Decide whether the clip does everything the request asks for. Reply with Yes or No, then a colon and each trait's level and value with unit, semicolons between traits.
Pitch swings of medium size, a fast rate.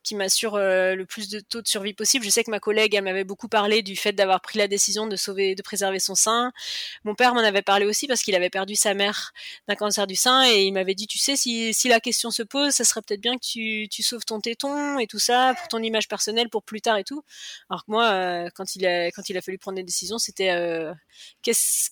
Yes: average, 3.0 semitones; fast, 270 wpm